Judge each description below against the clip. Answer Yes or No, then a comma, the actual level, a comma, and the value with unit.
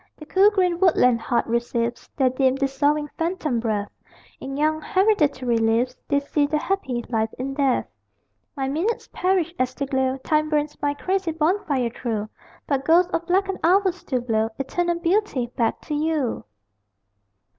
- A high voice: Yes, very high, 285 Hz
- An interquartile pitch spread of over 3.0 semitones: Yes, average, 5.3 semitones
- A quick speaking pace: No, average, 155 wpm